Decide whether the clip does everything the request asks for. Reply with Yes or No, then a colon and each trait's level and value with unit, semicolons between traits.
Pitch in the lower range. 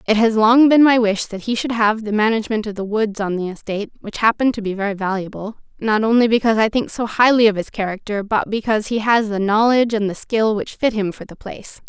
No: high, 215 Hz